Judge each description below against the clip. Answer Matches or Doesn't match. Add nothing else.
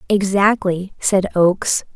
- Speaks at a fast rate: Doesn't match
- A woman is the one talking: Matches